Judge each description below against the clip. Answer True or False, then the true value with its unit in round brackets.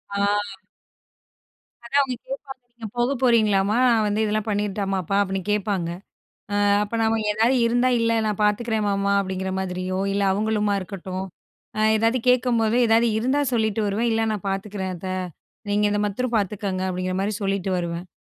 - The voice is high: True (210 Hz)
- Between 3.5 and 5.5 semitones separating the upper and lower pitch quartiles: False (3.0 semitones)